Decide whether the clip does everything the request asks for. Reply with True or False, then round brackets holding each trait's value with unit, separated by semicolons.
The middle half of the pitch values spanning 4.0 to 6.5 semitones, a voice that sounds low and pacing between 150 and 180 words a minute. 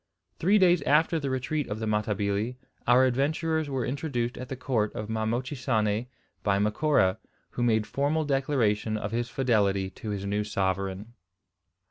True (4.7 semitones; 120 Hz; 155 wpm)